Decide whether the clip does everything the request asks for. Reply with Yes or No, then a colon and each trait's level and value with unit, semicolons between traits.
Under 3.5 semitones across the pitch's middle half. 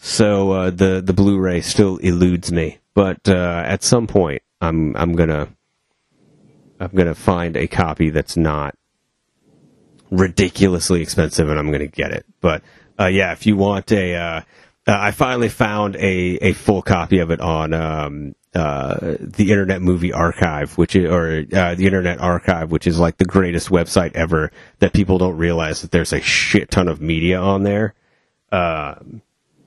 Yes: average, 2.9 semitones